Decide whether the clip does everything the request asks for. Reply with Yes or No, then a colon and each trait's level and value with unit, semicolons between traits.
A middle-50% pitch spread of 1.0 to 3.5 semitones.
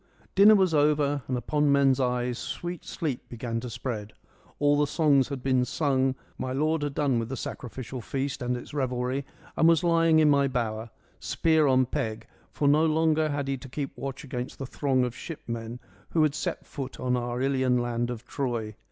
Yes: average, 3.1 semitones